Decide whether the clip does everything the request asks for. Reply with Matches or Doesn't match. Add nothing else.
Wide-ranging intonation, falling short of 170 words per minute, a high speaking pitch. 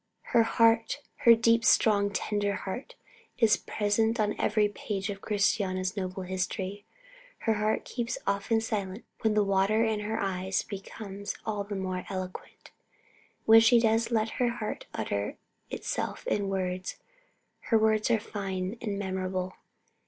Doesn't match